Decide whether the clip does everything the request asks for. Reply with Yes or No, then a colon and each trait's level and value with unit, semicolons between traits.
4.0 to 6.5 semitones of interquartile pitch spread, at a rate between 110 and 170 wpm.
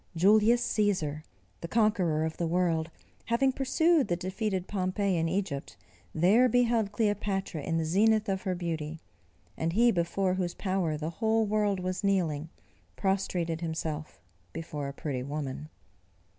Yes: average, 4.5 semitones; average, 145 wpm